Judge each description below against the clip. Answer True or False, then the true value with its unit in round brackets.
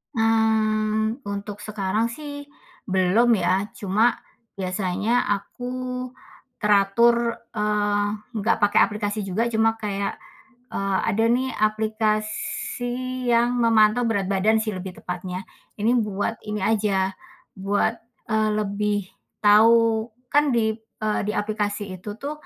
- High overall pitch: True (215 Hz)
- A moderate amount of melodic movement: False (1.9 semitones)